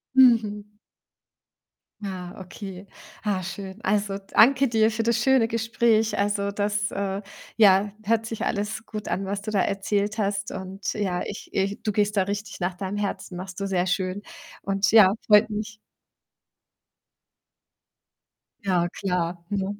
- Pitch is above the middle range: Yes, high, 205 Hz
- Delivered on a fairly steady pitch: Yes, narrow, 2.0 semitones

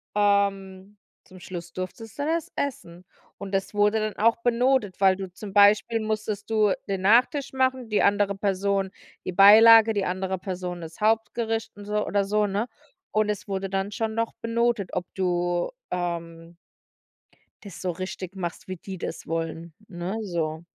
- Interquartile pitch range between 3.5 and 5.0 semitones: No, average, 2.9 semitones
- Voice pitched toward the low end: No, high, 200 Hz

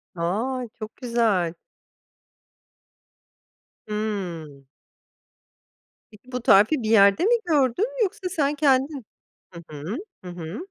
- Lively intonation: Yes, wide, 7.1 semitones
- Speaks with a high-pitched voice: Yes, high, 225 Hz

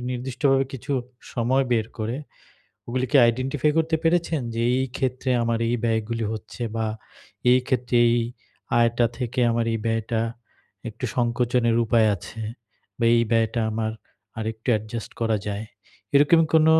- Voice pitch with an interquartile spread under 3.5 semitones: Yes, narrow, 2.5 semitones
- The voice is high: No, low, 120 Hz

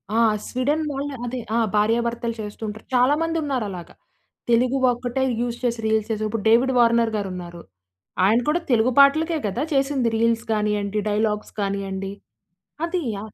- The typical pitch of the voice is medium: No, high, 230 Hz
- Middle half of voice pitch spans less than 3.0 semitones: No, average, 3.7 semitones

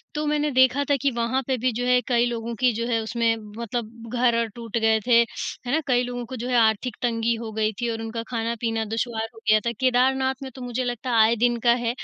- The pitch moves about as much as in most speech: No, narrow, 1.7 semitones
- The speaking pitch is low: No, high, 235 Hz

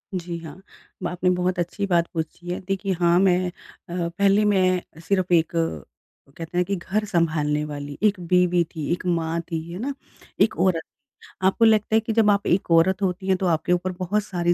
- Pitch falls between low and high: Yes, medium, 180 Hz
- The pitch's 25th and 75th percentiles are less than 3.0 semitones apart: Yes, narrow, 2.5 semitones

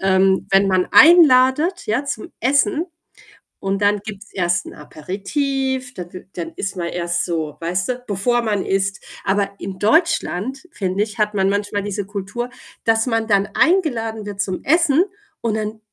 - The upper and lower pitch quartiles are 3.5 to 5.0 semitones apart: Yes, average, 4.6 semitones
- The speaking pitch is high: Yes, high, 205 Hz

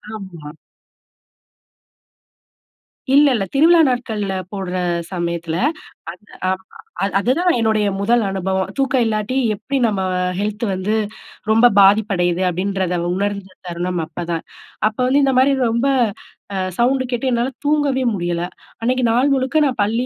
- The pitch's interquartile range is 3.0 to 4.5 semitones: No, average, 5.3 semitones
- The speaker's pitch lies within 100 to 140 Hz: No, high, 215 Hz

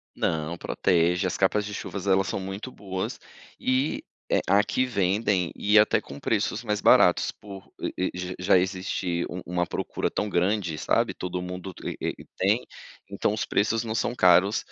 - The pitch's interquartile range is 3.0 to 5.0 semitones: No, narrow, 2.6 semitones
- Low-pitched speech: Yes, very low, 95 Hz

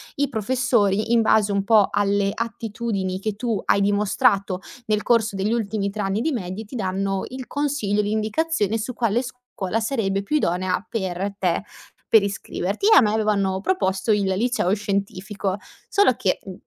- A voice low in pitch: No, high, 210 Hz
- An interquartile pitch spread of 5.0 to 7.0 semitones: No, average, 2.8 semitones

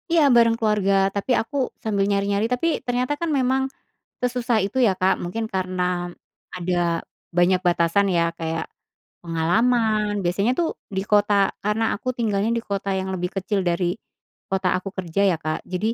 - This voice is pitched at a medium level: No, high, 200 Hz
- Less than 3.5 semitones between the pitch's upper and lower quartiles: No, average, 3.8 semitones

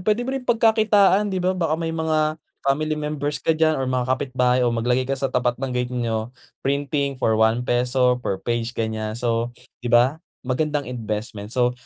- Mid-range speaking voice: No, low, 130 Hz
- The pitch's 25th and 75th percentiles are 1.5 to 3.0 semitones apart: No, average, 4.4 semitones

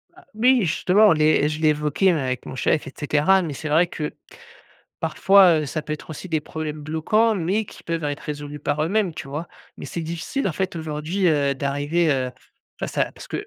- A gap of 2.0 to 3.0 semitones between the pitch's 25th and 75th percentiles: No, average, 3.5 semitones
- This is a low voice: No, medium, 155 Hz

